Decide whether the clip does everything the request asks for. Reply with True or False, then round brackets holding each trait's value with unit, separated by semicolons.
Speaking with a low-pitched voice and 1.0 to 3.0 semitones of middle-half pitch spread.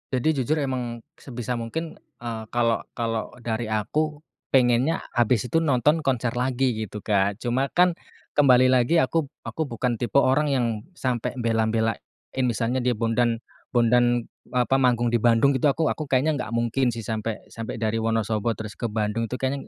True (120 Hz; 2.6 semitones)